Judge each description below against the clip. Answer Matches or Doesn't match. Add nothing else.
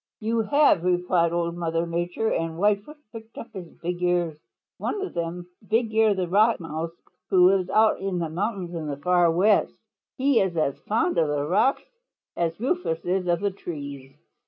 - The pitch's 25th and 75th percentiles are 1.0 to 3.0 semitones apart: Doesn't match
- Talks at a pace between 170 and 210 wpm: Matches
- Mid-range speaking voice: Matches